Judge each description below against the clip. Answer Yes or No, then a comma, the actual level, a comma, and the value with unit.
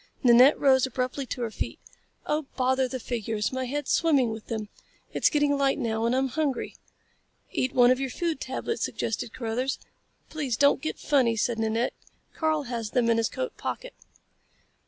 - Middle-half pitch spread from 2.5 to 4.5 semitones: Yes, average, 3.5 semitones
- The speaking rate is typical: Yes, average, 175 wpm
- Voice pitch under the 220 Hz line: No, very high, 255 Hz